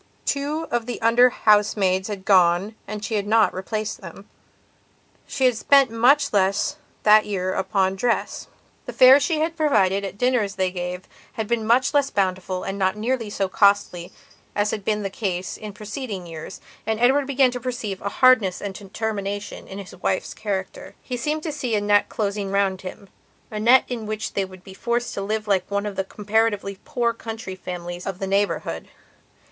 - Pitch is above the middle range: Yes, high, 210 Hz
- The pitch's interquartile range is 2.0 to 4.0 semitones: Yes, average, 3.5 semitones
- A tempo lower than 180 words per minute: No, average, 185 wpm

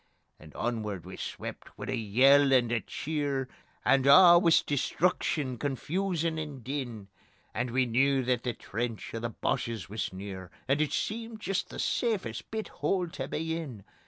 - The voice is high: No, low, 135 Hz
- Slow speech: No, average, 165 wpm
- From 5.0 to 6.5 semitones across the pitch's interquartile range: Yes, wide, 5.5 semitones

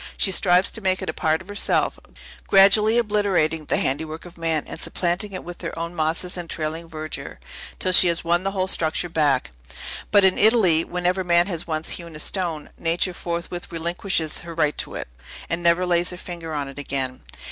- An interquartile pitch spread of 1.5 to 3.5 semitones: Yes, narrow, 2.5 semitones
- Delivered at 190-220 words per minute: Yes, average, 200 wpm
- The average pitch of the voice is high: No, medium, 170 Hz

